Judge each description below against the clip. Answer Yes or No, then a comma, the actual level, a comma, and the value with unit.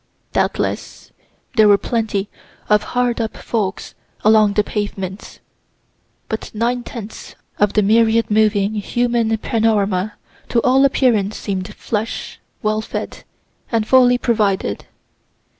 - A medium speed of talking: No, slow, 115 wpm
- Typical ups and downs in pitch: No, narrow, 2.1 semitones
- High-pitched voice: Yes, high, 215 Hz